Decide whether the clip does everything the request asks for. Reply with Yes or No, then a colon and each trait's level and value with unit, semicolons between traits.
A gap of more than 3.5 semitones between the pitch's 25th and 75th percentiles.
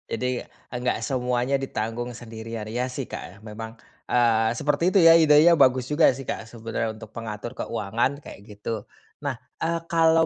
Yes: average, 4.1 semitones